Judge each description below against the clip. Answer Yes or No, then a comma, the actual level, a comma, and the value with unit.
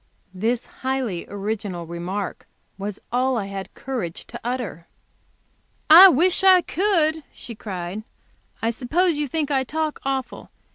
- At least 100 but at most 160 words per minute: Yes, slow, 135 wpm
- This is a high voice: Yes, high, 245 Hz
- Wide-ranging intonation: Yes, wide, 7.3 semitones